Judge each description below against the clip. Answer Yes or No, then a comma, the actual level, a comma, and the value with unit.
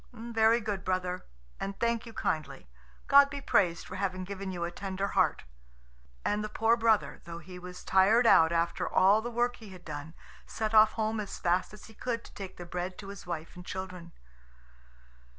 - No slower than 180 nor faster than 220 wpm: Yes, average, 195 wpm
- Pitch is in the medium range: No, high, 195 Hz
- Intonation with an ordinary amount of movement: Yes, average, 3.6 semitones